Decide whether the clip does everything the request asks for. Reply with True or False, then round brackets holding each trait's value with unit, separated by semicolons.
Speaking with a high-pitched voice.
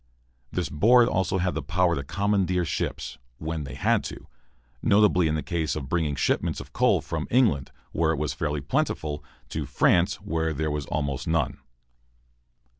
False (80 Hz)